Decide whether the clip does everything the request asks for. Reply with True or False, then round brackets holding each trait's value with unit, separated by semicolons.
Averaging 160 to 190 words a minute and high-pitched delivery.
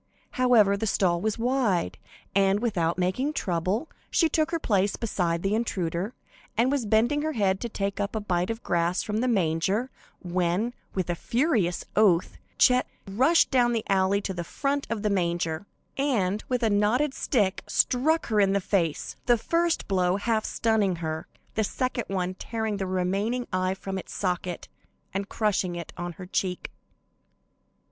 True (170 wpm; 200 Hz)